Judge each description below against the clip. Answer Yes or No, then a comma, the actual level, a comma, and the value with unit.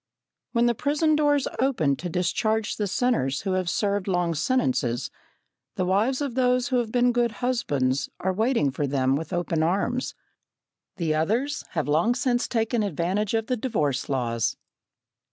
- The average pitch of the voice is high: Yes, high, 205 Hz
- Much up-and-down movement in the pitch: Yes, wide, 7.6 semitones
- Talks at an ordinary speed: Yes, average, 160 wpm